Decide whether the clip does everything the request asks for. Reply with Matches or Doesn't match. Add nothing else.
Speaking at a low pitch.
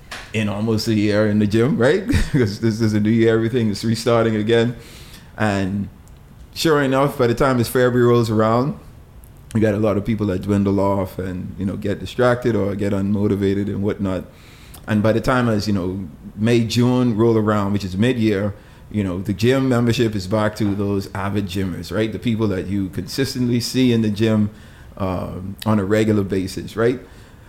Matches